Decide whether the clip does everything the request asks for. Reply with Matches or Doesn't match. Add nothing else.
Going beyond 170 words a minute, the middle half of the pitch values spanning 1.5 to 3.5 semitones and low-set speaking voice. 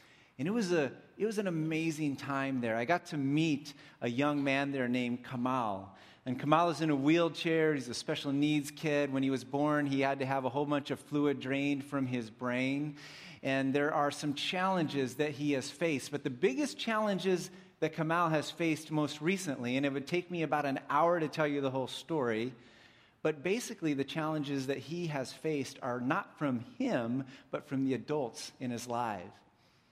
Doesn't match